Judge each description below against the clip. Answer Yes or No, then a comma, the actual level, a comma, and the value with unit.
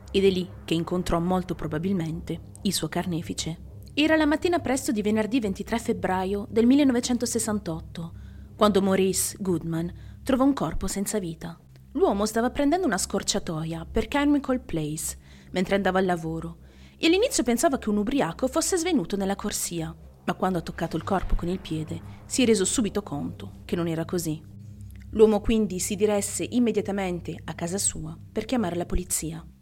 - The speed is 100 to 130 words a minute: No, average, 160 wpm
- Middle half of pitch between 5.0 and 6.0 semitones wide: Yes, wide, 5.6 semitones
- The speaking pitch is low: No, high, 195 Hz